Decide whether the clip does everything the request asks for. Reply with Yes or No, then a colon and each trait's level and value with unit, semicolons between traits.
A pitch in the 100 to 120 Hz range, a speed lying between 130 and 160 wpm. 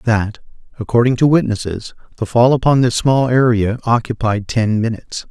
Yes: low, 115 Hz; average, 145 wpm